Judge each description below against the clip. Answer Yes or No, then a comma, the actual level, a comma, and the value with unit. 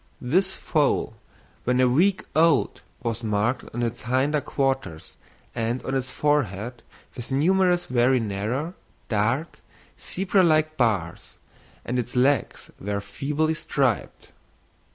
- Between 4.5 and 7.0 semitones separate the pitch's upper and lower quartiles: Yes, average, 4.8 semitones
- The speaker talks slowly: Yes, slow, 120 wpm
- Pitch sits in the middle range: No, low, 130 Hz